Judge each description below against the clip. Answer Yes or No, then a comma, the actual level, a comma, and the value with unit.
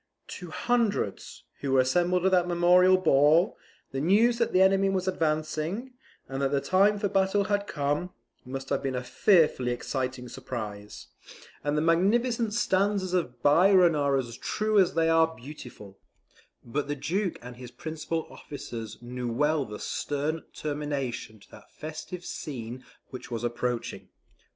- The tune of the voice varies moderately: No, wide, 6.2 semitones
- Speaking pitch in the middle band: Yes, medium, 155 Hz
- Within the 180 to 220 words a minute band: No, average, 155 wpm